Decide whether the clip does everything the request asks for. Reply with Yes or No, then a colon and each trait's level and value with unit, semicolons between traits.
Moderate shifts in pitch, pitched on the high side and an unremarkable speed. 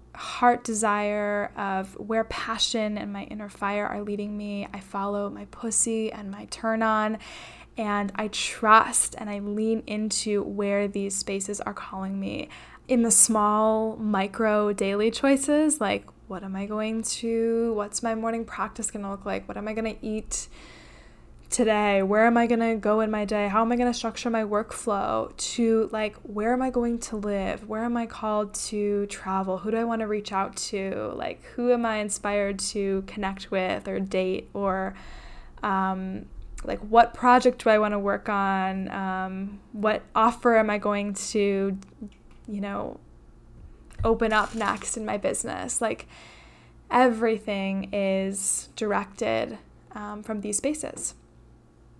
No: narrow, 2.1 semitones; high, 210 Hz; average, 165 wpm